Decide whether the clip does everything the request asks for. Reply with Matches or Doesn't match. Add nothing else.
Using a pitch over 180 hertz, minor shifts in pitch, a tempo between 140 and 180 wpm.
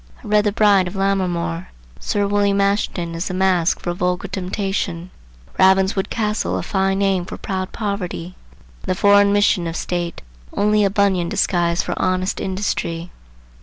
Matches